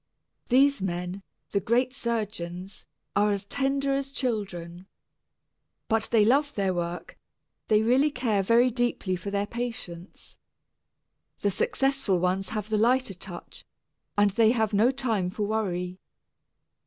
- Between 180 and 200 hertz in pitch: No, high, 210 Hz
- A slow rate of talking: Yes, slow, 130 wpm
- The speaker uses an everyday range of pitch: Yes, average, 4.6 semitones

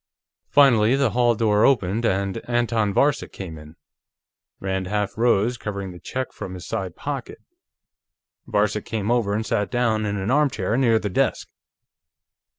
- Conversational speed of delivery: Yes, average, 155 wpm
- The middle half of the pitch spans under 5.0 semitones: Yes, average, 3.5 semitones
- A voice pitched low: Yes, low, 105 Hz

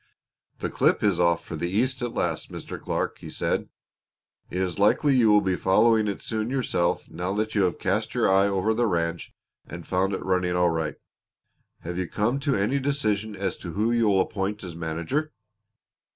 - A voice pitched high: No, low, 100 Hz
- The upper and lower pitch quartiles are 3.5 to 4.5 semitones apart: Yes, average, 3.9 semitones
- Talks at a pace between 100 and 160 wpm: No, average, 195 wpm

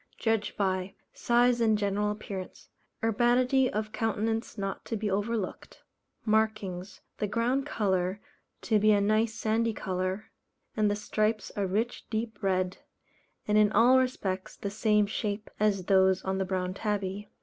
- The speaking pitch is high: Yes, high, 210 Hz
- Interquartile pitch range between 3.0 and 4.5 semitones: No, narrow, 2.4 semitones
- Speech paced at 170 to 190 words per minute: No, average, 150 wpm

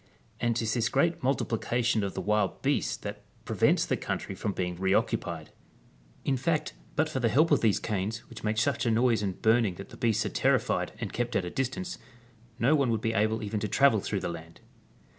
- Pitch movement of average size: Yes, average, 3.5 semitones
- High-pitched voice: No, low, 115 Hz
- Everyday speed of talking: No, fast, 210 wpm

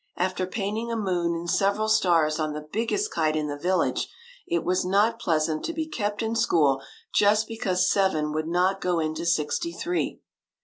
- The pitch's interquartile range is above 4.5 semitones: Yes, wide, 5.5 semitones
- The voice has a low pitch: No, medium, 185 Hz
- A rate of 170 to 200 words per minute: Yes, average, 185 wpm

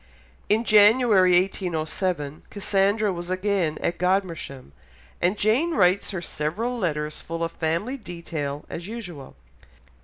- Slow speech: Yes, slow, 120 wpm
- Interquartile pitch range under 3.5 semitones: No, average, 4.0 semitones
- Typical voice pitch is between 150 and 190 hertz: Yes, medium, 185 Hz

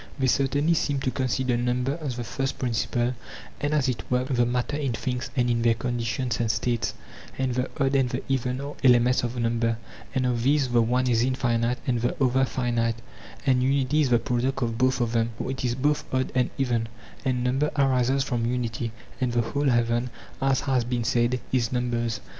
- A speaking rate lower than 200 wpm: No, fast, 205 wpm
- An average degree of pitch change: No, narrow, 1.8 semitones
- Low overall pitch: Yes, low, 125 Hz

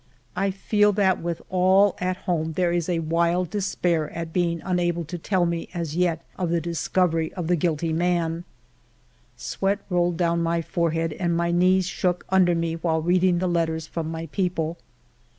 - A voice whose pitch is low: No, medium, 175 Hz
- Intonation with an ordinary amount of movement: No, narrow, 1.7 semitones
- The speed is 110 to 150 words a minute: No, average, 170 wpm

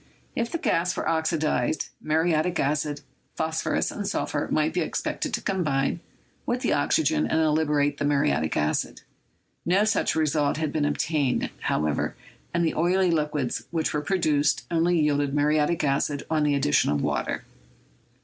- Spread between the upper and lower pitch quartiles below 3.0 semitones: Yes, narrow, 2.4 semitones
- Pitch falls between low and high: Yes, medium, 155 Hz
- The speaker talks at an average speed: Yes, average, 155 wpm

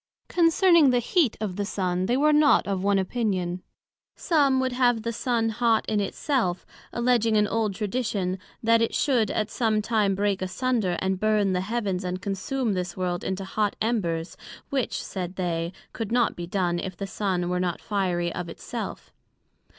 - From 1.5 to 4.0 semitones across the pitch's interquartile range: No, average, 4.4 semitones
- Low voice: No, high, 205 Hz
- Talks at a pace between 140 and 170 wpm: No, average, 180 wpm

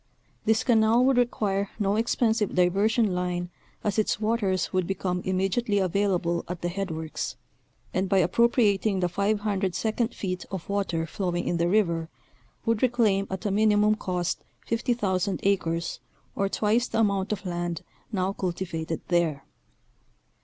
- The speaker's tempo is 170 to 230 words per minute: No, average, 145 wpm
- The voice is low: No, high, 195 Hz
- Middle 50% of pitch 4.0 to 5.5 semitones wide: No, average, 3.3 semitones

